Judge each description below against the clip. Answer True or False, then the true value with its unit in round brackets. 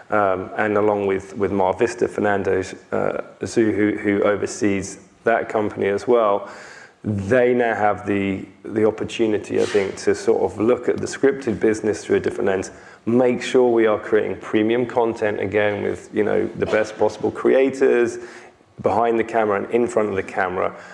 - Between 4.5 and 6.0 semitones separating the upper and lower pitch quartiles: False (3.1 semitones)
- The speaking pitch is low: True (110 Hz)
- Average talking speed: True (170 wpm)